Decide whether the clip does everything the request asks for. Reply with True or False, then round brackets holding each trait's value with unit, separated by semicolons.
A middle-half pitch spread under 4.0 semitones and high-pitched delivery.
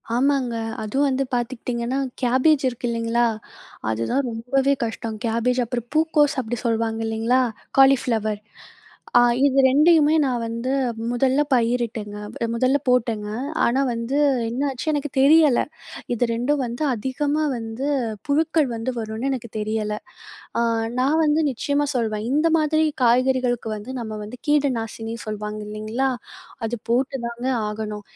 True (3.2 semitones; 245 Hz)